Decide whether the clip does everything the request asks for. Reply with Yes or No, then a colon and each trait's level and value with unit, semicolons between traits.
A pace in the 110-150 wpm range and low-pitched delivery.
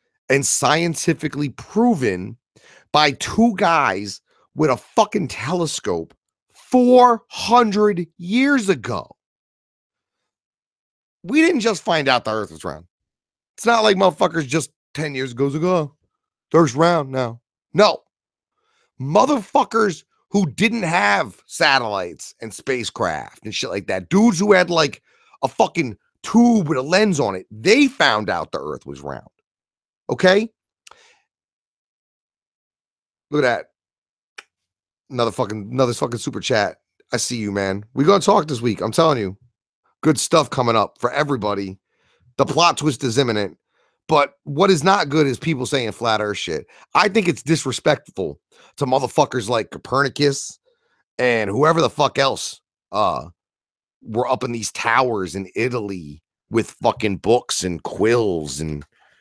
No: average, 140 wpm; medium, 145 Hz